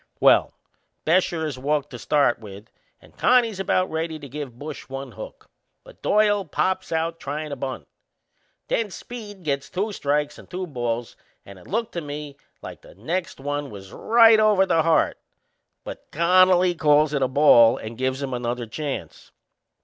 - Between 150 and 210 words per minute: Yes, average, 170 wpm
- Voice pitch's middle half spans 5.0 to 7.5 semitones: Yes, wide, 5.5 semitones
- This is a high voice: No, medium, 150 Hz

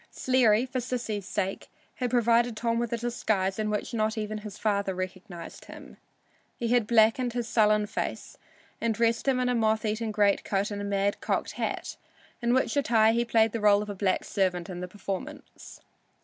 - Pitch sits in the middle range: No, high, 220 Hz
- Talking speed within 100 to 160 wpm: No, average, 190 wpm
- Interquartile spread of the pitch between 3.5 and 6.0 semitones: No, narrow, 2.6 semitones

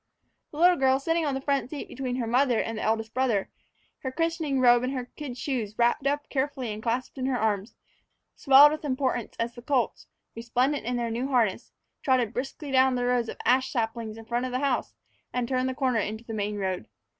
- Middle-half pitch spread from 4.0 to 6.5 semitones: No, average, 2.8 semitones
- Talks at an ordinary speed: No, fast, 215 wpm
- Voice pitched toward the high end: Yes, very high, 250 Hz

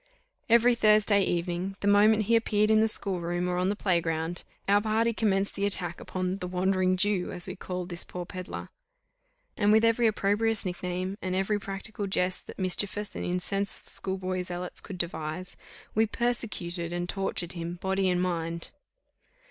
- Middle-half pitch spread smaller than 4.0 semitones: Yes, narrow, 2.6 semitones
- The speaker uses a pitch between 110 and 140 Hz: No, high, 190 Hz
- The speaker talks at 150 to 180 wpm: Yes, average, 170 wpm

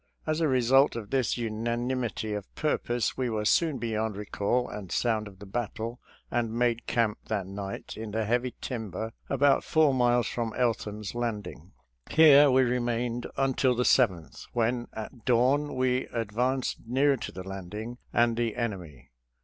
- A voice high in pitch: No, low, 120 Hz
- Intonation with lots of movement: No, average, 2.9 semitones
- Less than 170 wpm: Yes, average, 160 wpm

